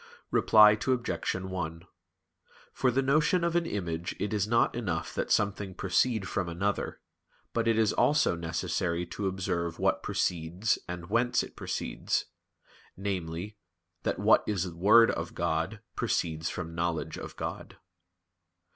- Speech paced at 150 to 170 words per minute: No, average, 140 wpm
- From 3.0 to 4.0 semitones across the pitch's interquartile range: No, average, 4.6 semitones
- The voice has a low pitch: Yes, very low, 95 Hz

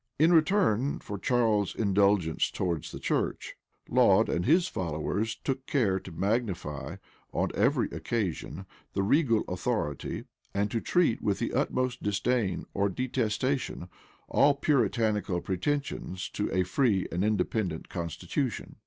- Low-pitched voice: Yes, low, 105 Hz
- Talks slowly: Yes, slow, 125 wpm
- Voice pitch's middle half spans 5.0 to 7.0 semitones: Yes, wide, 5.4 semitones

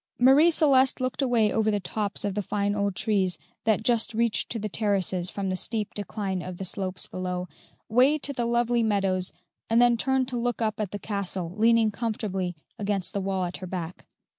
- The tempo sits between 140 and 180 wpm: No, average, 200 wpm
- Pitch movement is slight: No, average, 3.7 semitones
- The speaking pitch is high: Yes, high, 210 Hz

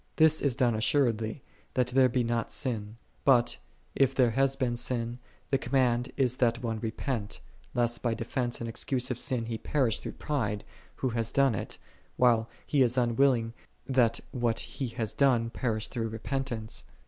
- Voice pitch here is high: No, low, 120 Hz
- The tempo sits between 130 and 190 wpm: Yes, average, 170 wpm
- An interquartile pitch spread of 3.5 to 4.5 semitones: No, narrow, 2.4 semitones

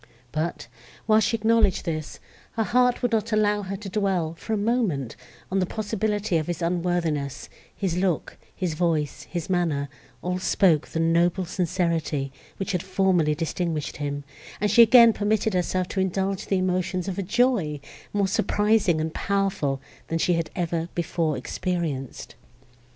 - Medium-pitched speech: Yes, medium, 180 Hz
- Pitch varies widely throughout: No, average, 3.8 semitones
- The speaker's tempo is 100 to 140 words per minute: No, average, 155 wpm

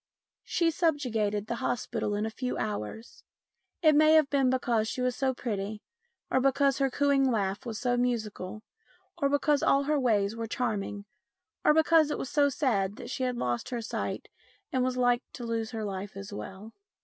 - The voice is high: Yes, high, 245 Hz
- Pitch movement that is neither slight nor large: Yes, average, 4.4 semitones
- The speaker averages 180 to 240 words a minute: Yes, average, 185 wpm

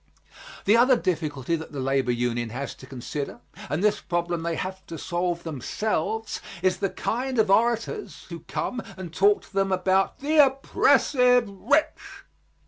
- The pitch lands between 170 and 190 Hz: Yes, medium, 185 Hz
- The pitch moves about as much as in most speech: No, wide, 6.5 semitones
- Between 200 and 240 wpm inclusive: No, average, 155 wpm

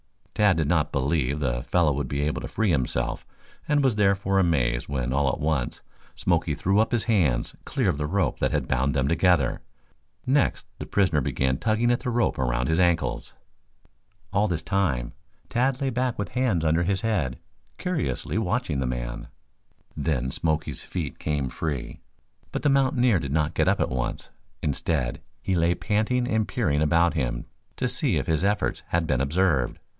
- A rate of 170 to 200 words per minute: Yes, average, 180 wpm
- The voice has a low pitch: Yes, very low, 80 Hz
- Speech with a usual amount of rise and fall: No, wide, 7.3 semitones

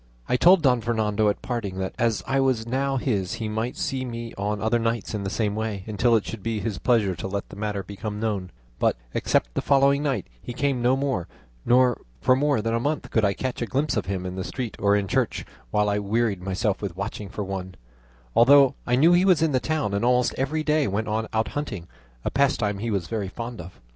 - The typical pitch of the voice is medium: No, low, 115 Hz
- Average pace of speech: No, fast, 235 wpm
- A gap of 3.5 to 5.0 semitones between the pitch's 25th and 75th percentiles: Yes, average, 4.2 semitones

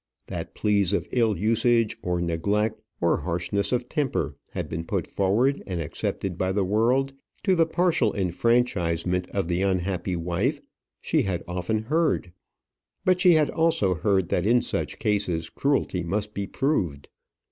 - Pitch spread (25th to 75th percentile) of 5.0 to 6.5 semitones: Yes, average, 5.3 semitones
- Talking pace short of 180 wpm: Yes, average, 155 wpm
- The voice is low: Yes, low, 100 Hz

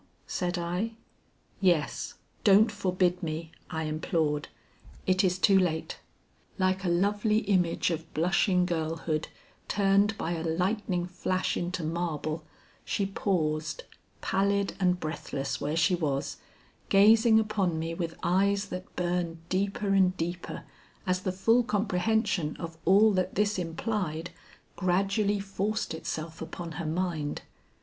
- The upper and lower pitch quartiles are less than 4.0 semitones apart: Yes, average, 3.2 semitones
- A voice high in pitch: No, medium, 180 Hz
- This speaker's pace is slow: Yes, slow, 125 wpm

